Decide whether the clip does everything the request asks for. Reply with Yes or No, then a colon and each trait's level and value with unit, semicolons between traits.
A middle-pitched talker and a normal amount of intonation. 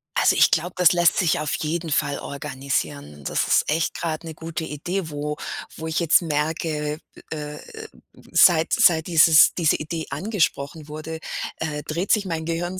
No: medium, 160 Hz; narrow, 2.1 semitones